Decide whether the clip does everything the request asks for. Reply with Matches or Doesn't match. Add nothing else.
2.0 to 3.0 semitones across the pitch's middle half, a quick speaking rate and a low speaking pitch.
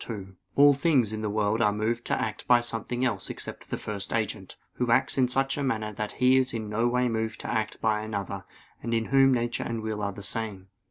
Matches